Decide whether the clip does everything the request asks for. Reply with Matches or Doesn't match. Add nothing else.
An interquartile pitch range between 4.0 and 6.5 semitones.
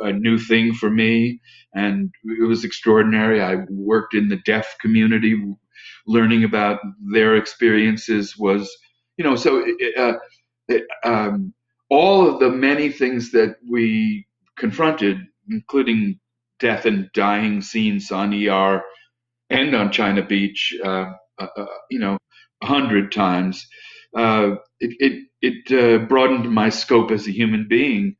Doesn't match